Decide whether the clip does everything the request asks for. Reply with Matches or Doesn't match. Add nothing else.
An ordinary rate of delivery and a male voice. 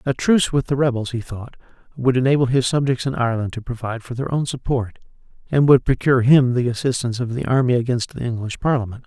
Doesn't match